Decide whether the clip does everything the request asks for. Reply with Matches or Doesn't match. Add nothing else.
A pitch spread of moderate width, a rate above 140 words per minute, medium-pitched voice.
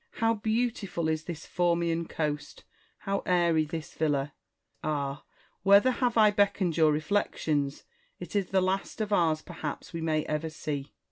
Matches